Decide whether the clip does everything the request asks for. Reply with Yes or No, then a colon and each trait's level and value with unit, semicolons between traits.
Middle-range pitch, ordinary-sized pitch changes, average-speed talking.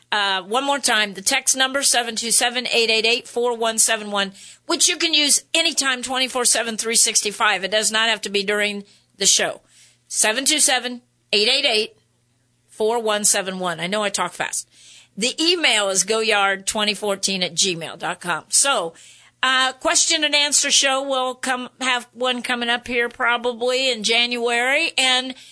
No: high, 235 Hz; average, 3.8 semitones; average, 145 wpm